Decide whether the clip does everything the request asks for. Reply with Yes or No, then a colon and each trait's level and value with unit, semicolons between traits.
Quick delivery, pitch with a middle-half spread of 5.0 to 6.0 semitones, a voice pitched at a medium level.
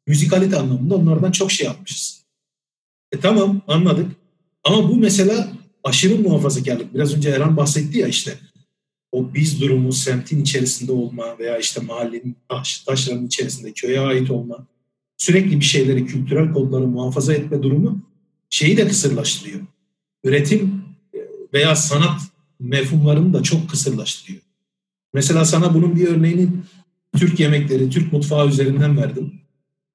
No: average, 130 wpm; average, 5.3 semitones; medium, 150 Hz